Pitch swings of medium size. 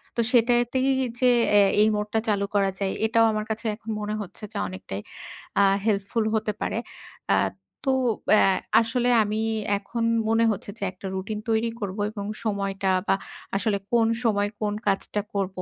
No: narrow, 2.3 semitones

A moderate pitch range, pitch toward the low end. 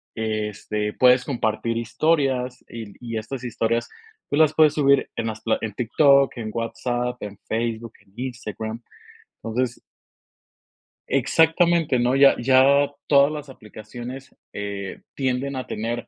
Yes: average, 3.5 semitones; low, 120 Hz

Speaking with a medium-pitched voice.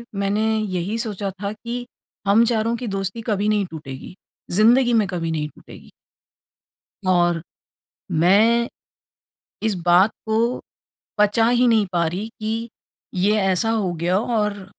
No: high, 210 Hz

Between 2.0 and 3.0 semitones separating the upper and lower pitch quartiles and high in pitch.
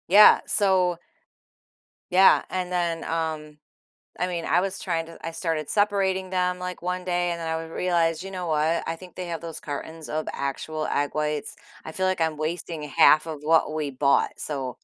No: average, 2.7 semitones; medium, 165 Hz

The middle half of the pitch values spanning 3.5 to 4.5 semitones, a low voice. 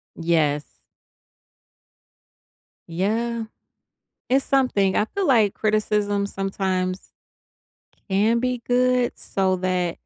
No: average, 4.2 semitones; high, 205 Hz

